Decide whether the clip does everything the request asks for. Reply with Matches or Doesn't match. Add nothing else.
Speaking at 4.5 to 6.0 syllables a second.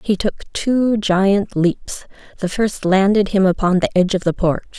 Matches